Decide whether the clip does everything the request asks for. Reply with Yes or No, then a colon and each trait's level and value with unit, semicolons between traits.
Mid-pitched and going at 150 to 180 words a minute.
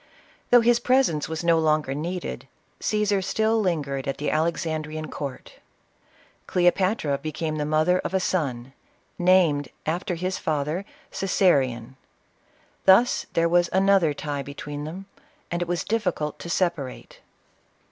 No: medium, 165 Hz; slow, 135 wpm